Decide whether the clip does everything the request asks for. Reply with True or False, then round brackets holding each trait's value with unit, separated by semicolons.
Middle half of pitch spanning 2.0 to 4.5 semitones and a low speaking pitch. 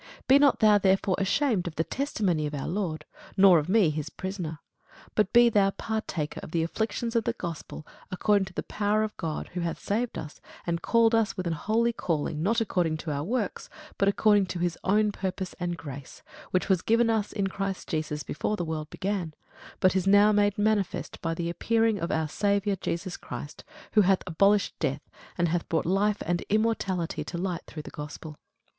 False (4.2 semitones; 190 Hz)